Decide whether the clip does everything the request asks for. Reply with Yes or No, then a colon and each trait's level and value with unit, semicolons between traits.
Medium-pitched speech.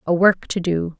Yes: medium, 175 Hz